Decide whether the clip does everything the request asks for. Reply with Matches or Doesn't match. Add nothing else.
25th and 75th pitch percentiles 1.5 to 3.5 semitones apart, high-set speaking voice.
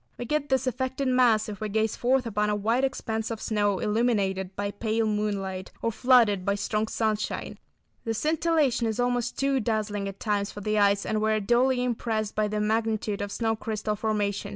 Matches